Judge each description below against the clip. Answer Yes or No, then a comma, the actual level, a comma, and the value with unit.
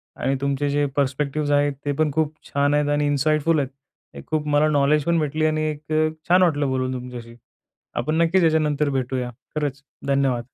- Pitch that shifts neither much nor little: No, narrow, 1.9 semitones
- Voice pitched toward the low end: No, medium, 145 Hz